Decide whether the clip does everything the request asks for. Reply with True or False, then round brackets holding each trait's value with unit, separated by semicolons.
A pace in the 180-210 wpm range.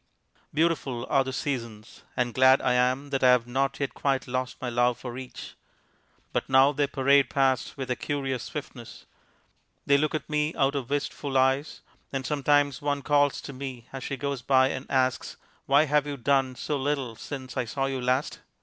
True (190 wpm)